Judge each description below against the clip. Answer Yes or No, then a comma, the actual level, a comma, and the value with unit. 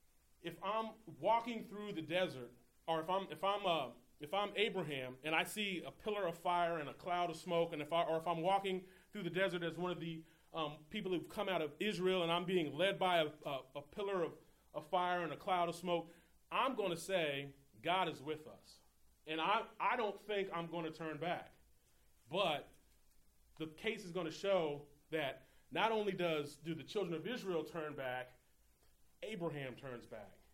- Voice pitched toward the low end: No, medium, 170 Hz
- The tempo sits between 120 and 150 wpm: No, fast, 205 wpm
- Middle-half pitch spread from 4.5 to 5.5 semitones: No, average, 3.7 semitones